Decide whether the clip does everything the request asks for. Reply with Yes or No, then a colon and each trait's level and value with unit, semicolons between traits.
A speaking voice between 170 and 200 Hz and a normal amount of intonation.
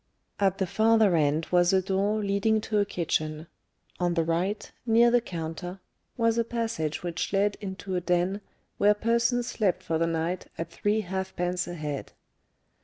Yes: high, 190 Hz; average, 3.9 semitones